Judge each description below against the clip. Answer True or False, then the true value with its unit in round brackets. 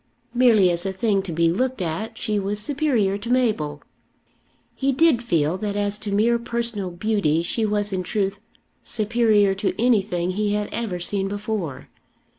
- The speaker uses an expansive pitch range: False (3.3 semitones)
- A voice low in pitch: False (205 Hz)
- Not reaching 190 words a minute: True (165 wpm)